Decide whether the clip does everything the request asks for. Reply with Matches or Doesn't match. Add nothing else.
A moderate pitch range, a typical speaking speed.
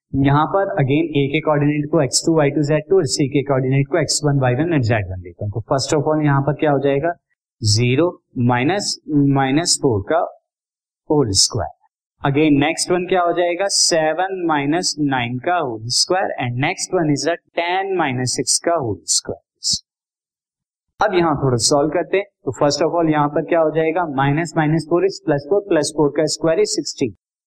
Matches